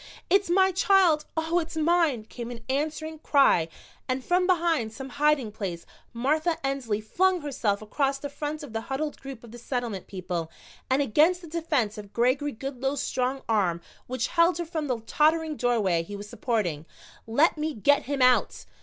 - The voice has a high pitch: Yes, very high, 275 Hz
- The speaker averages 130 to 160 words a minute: No, average, 175 wpm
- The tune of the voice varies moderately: No, wide, 5.8 semitones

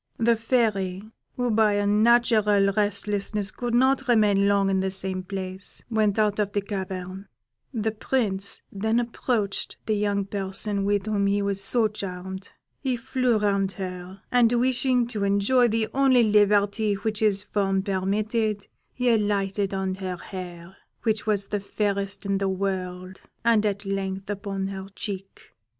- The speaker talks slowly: No, average, 155 wpm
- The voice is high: Yes, high, 205 Hz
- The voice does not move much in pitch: Yes, narrow, 2.1 semitones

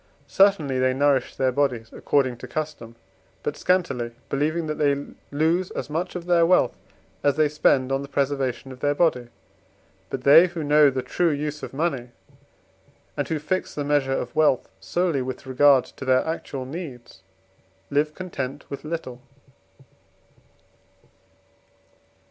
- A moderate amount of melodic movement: Yes, average, 3.3 semitones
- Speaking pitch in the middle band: Yes, medium, 145 Hz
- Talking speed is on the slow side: No, average, 150 wpm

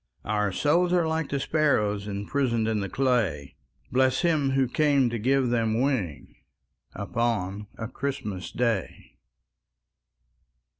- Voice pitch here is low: Yes, low, 120 Hz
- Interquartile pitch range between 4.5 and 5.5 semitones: Yes, average, 5.0 semitones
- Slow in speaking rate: Yes, slow, 120 wpm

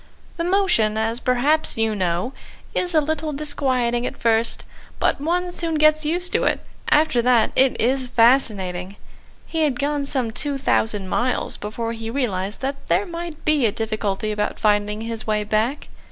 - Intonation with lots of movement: Yes, wide, 5.7 semitones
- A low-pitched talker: No, high, 245 Hz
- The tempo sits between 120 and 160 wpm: No, average, 170 wpm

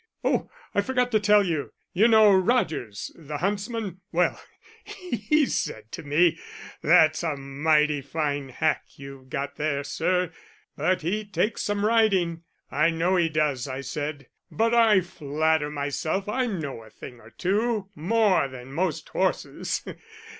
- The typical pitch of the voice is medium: Yes, medium, 165 Hz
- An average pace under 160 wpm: Yes, average, 145 wpm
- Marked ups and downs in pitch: Yes, wide, 6.2 semitones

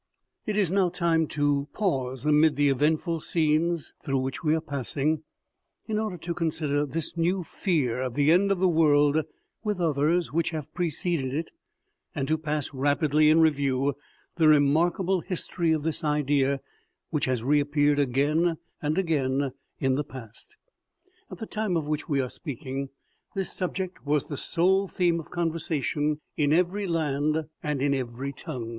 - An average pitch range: Yes, average, 3.2 semitones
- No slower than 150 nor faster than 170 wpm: Yes, average, 165 wpm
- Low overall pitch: No, medium, 155 Hz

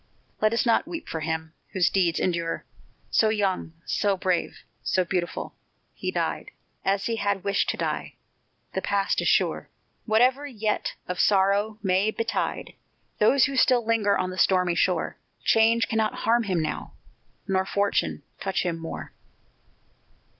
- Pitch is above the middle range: Yes, high, 200 Hz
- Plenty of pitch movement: No, average, 3.3 semitones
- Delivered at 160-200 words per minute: No, average, 150 wpm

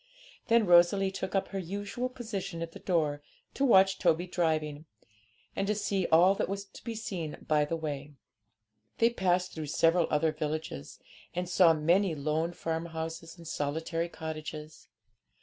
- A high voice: No, medium, 170 Hz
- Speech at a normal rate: Yes, average, 155 wpm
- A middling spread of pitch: Yes, average, 3.6 semitones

